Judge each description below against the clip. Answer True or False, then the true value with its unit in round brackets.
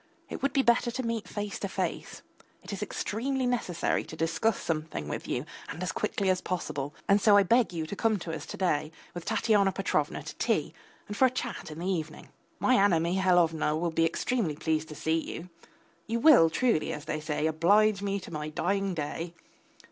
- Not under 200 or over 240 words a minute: True (205 wpm)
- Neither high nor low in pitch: True (180 Hz)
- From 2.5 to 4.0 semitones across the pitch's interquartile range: False (5.0 semitones)